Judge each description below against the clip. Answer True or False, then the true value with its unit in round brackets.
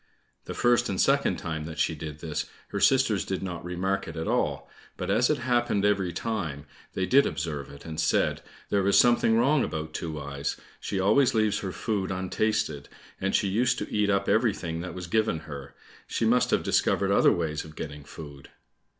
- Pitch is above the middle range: False (95 Hz)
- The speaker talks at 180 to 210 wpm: True (195 wpm)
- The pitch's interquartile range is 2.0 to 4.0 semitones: False (5.6 semitones)